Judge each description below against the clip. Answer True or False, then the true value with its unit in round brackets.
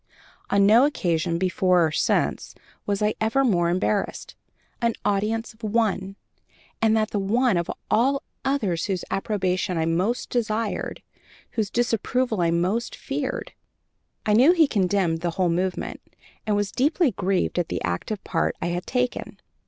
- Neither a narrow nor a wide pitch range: True (4.2 semitones)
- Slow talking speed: False (150 wpm)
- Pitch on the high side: True (205 Hz)